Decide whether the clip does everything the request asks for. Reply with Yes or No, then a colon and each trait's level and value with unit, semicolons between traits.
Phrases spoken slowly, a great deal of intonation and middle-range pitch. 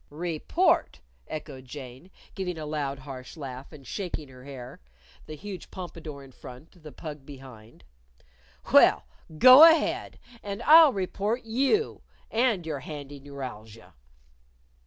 Yes: slow, 125 wpm; wide, 6.1 semitones; medium, 150 Hz